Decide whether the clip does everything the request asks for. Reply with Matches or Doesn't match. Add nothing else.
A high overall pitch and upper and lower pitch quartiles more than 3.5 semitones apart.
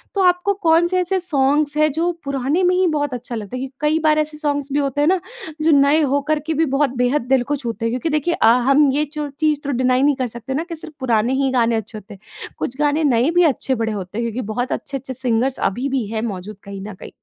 Matches